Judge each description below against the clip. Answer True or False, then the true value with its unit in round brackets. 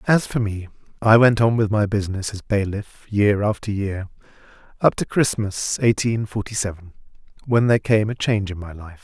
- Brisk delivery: False (185 wpm)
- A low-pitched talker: True (105 Hz)